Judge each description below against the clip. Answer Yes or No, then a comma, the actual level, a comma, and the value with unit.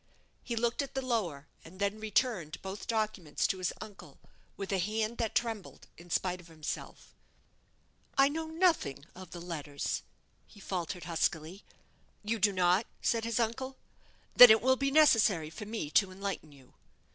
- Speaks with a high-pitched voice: Yes, high, 205 Hz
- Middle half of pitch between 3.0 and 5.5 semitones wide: Yes, average, 5.0 semitones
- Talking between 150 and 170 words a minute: Yes, average, 165 wpm